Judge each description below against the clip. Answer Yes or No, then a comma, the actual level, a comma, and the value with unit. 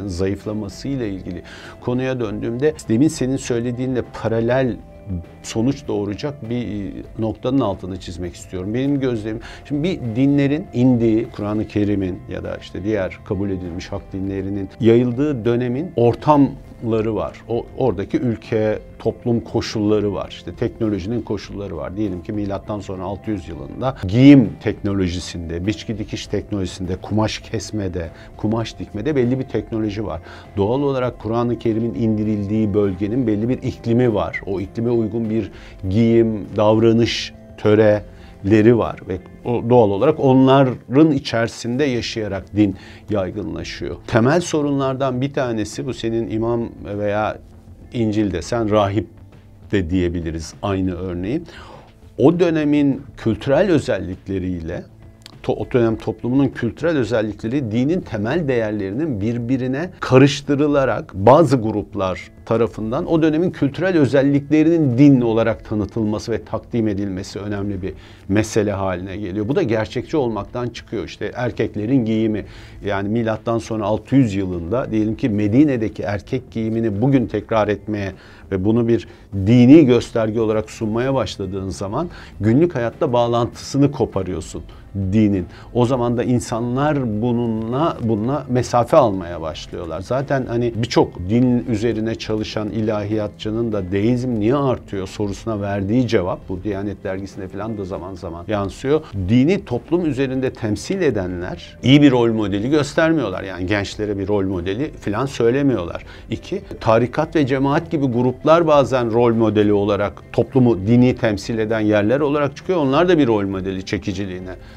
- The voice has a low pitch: Yes, low, 110 Hz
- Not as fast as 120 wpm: No, average, 130 wpm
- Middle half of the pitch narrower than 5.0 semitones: Yes, average, 3.5 semitones